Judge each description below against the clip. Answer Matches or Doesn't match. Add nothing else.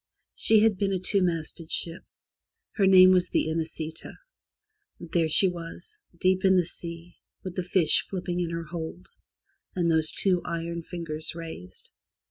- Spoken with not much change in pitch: Matches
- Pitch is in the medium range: Matches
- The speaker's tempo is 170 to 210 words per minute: Doesn't match